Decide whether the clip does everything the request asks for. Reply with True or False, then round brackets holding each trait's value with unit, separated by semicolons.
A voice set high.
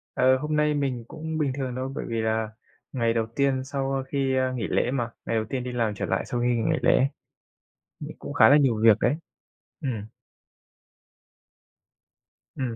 False (130 Hz)